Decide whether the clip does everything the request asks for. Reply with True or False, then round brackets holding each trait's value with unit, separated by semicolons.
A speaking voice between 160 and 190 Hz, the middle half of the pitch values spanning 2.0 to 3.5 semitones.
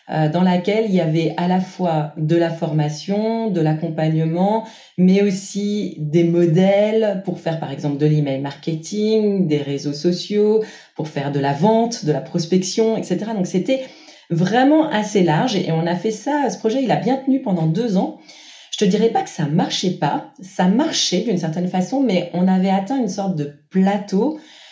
False (185 Hz; 4.9 semitones)